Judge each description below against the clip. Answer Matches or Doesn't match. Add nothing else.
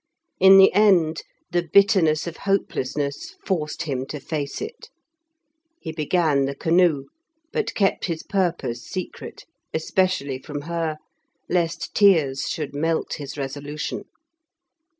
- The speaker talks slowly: Matches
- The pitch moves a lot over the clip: Doesn't match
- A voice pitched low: Doesn't match